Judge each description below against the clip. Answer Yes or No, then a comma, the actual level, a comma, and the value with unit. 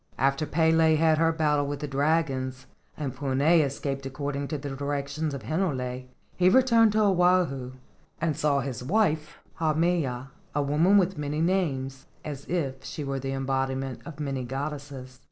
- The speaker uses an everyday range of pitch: Yes, average, 3.2 semitones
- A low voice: No, medium, 145 Hz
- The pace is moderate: Yes, average, 160 wpm